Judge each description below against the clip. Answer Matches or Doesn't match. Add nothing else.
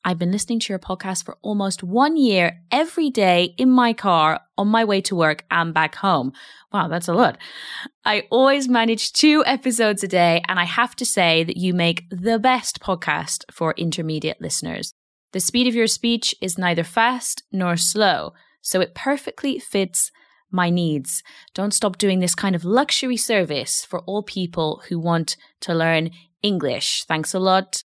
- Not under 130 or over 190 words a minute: Matches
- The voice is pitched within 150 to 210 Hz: Matches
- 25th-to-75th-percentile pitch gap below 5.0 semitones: Doesn't match